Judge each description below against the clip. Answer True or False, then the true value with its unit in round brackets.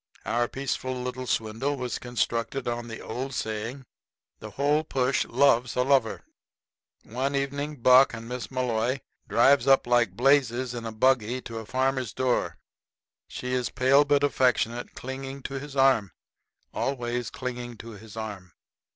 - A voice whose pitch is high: False (125 Hz)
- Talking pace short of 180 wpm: True (150 wpm)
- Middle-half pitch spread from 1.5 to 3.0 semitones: True (2.5 semitones)